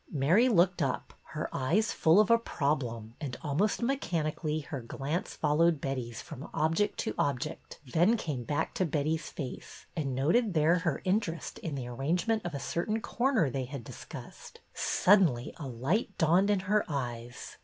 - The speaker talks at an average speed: Yes, average, 170 wpm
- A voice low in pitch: No, medium, 155 Hz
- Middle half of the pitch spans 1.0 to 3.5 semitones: No, wide, 5.5 semitones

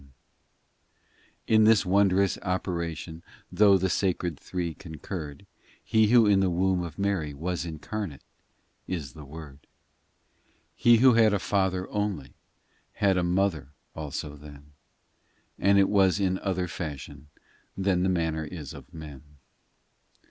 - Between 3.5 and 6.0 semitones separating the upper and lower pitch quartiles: Yes, average, 4.0 semitones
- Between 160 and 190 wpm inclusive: No, slow, 135 wpm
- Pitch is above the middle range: No, very low, 90 Hz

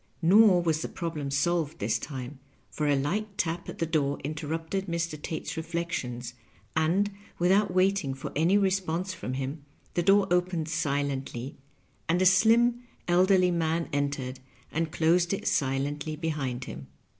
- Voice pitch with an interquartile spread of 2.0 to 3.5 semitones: No, average, 4.1 semitones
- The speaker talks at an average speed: Yes, average, 150 wpm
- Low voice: No, medium, 165 Hz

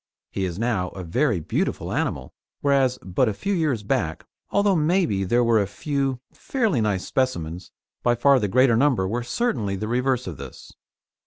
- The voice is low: Yes, low, 120 Hz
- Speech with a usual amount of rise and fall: No, wide, 6.0 semitones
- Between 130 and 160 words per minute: No, average, 175 wpm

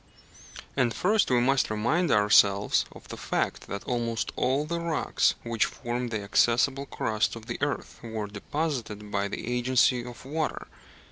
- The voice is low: Yes, low, 120 Hz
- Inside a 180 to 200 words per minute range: No, average, 155 wpm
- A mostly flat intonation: No, average, 4.2 semitones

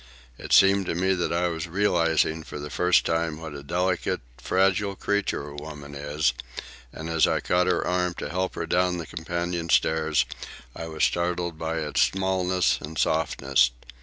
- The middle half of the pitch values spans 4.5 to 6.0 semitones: No, narrow, 2.5 semitones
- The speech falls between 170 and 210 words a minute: Yes, average, 175 wpm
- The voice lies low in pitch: Yes, very low, 85 Hz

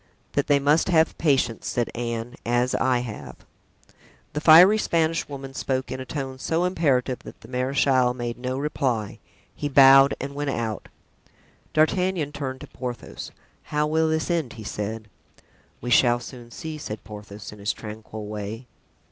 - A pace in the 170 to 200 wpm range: No, average, 160 wpm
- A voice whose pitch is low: Yes, low, 130 Hz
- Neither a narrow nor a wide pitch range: Yes, average, 4.0 semitones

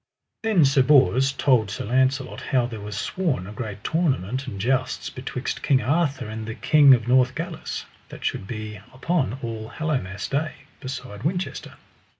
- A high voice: No, low, 130 Hz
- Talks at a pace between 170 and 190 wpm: No, average, 155 wpm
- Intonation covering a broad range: No, average, 4.4 semitones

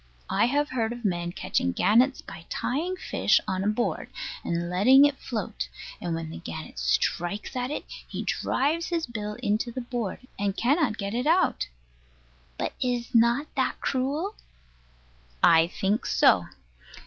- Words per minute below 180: Yes, average, 160 wpm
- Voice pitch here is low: No, high, 235 Hz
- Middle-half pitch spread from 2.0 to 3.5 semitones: No, wide, 5.5 semitones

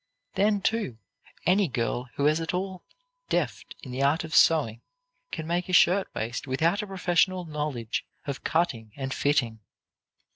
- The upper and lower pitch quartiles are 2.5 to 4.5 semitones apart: No, wide, 5.6 semitones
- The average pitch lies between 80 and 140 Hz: No, medium, 155 Hz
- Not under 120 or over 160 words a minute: Yes, average, 155 wpm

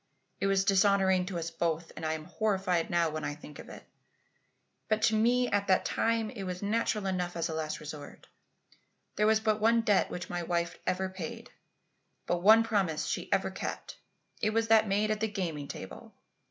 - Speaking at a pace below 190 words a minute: No, average, 195 wpm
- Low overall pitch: No, high, 190 Hz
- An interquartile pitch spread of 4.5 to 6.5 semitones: No, average, 4.1 semitones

